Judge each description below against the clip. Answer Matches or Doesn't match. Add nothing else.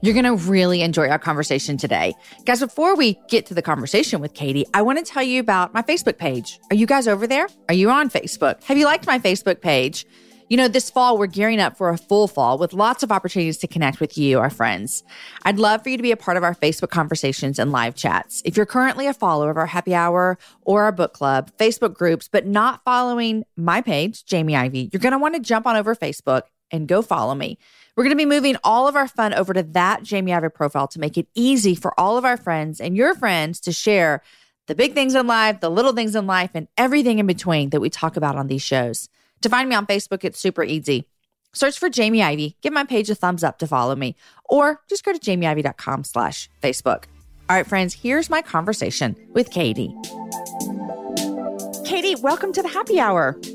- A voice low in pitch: Doesn't match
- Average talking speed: Doesn't match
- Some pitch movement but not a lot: Doesn't match